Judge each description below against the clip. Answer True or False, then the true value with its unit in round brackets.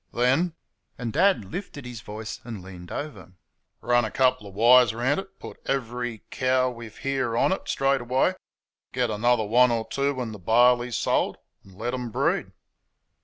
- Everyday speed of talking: True (170 wpm)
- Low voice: True (120 Hz)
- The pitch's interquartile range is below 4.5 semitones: True (2.8 semitones)